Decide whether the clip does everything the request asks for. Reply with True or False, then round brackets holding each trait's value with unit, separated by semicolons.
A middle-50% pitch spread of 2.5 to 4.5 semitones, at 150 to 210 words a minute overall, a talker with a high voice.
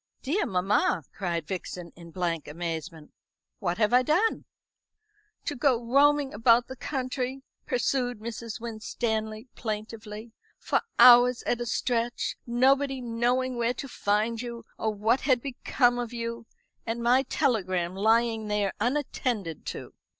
False (3.2 semitones; 135 wpm; 235 Hz)